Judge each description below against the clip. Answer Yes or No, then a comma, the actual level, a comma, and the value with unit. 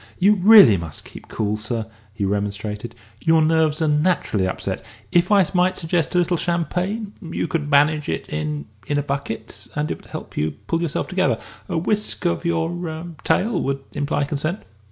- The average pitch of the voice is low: No, medium, 155 Hz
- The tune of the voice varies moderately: No, wide, 7.3 semitones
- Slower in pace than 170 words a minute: No, average, 185 wpm